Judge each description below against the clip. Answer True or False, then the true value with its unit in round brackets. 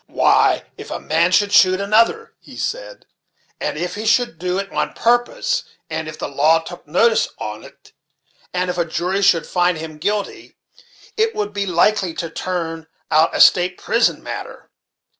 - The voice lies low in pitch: False (180 Hz)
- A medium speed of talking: True (170 wpm)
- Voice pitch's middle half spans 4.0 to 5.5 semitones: True (4.4 semitones)